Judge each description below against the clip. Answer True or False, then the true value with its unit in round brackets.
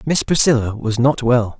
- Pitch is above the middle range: False (125 Hz)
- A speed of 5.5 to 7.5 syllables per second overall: False (4.8 syllables/s)